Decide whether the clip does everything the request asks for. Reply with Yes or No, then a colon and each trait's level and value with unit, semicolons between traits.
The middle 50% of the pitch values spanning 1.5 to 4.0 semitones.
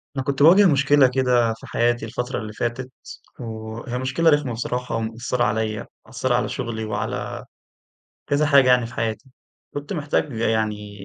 Yes: average, 3.4 semitones